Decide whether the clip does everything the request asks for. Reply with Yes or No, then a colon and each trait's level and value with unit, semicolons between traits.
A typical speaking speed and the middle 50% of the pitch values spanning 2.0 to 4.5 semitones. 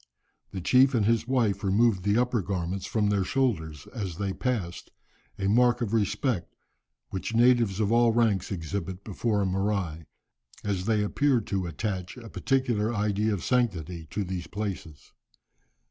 Yes: average, 155 wpm; average, 3.8 semitones